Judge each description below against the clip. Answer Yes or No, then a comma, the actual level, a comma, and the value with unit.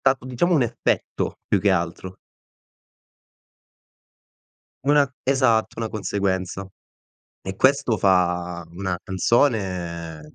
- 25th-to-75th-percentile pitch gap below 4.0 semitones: No, wide, 5.7 semitones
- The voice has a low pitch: Yes, low, 100 Hz